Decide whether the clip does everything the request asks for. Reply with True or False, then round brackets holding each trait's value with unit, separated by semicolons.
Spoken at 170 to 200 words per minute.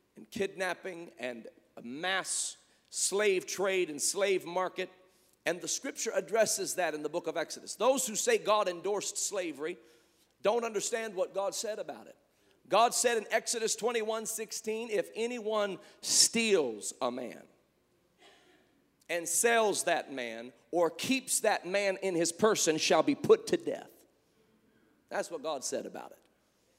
False (145 wpm)